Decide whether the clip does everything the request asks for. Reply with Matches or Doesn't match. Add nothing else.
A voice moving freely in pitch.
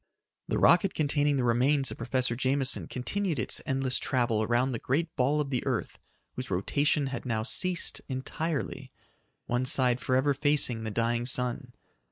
Doesn't match